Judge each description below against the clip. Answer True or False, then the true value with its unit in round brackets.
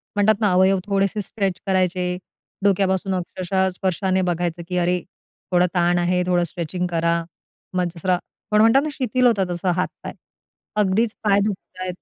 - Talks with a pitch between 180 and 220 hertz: True (185 Hz)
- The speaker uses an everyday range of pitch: False (2.0 semitones)